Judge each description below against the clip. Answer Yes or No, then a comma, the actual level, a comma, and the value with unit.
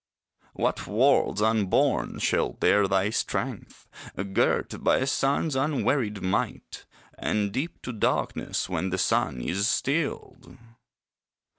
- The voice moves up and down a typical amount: No, wide, 5.8 semitones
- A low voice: Yes, low, 105 Hz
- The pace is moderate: No, slow, 115 wpm